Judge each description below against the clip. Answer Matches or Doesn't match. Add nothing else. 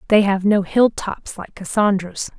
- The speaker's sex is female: Matches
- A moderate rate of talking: Matches